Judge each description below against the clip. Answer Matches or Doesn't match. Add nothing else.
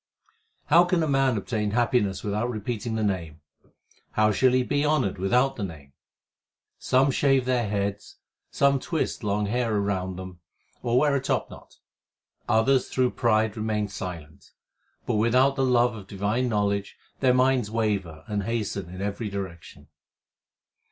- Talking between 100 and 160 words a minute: Matches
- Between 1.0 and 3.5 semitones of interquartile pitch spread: Doesn't match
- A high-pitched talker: Doesn't match